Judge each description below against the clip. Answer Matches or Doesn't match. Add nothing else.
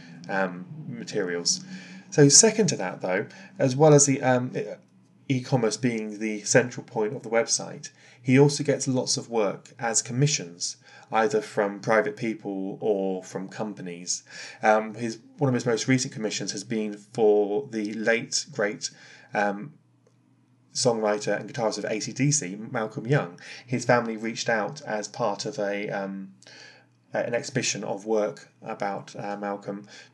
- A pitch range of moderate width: Matches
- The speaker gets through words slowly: Doesn't match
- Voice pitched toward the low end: Matches